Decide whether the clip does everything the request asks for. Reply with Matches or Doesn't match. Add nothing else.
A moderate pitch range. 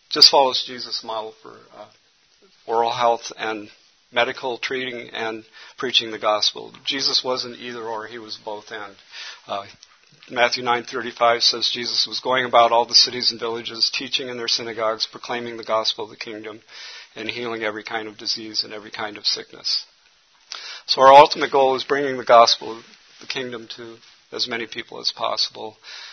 Doesn't match